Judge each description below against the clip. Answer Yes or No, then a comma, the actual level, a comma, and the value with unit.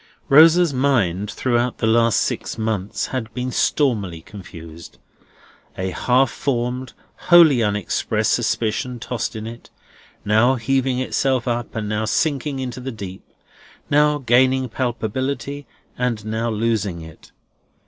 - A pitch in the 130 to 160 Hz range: No, low, 120 Hz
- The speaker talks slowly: Yes, slow, 125 wpm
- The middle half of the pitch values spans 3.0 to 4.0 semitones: Yes, average, 3.4 semitones